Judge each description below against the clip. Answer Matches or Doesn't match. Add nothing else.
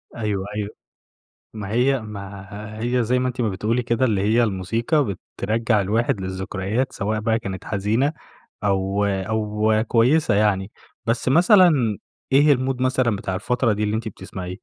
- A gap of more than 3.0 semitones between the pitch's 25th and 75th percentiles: Matches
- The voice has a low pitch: Matches